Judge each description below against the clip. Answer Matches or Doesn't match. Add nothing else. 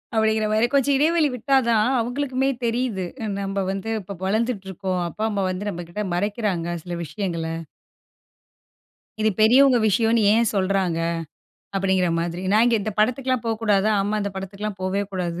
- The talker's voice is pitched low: Doesn't match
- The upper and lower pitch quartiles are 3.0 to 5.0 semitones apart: Matches